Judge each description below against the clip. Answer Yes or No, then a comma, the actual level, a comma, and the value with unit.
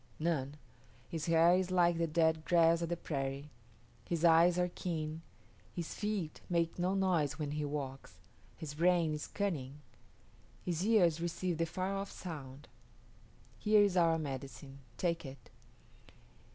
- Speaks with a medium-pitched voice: Yes, medium, 165 Hz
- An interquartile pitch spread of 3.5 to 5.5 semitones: No, average, 3.0 semitones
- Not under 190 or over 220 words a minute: No, average, 145 wpm